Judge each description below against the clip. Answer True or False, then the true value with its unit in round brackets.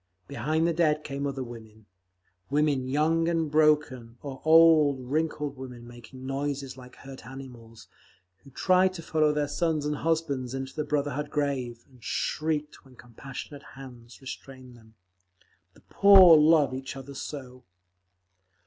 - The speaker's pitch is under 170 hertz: True (140 Hz)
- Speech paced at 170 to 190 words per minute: False (140 wpm)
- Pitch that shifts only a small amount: False (3.2 semitones)